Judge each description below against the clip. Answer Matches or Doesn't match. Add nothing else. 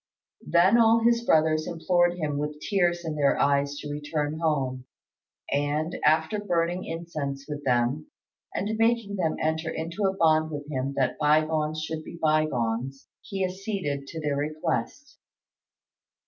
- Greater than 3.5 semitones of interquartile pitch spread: Doesn't match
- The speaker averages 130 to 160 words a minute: Matches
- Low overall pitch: Doesn't match